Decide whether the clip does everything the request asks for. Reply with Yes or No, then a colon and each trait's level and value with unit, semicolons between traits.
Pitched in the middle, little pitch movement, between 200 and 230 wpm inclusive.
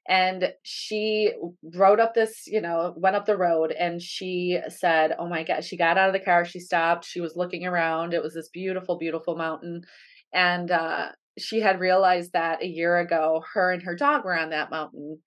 Yes: medium, 175 Hz; narrow, 2.0 semitones; fast, 205 wpm